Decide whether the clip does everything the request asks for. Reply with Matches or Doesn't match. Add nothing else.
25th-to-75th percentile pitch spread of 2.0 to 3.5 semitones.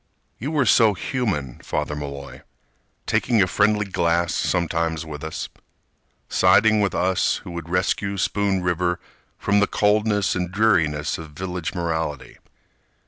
Doesn't match